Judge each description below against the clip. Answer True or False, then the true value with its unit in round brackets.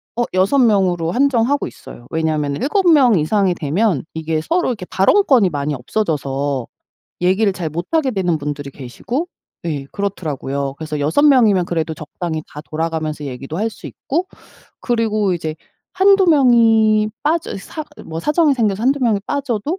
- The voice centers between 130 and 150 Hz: False (195 Hz)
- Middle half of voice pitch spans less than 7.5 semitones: False (8.2 semitones)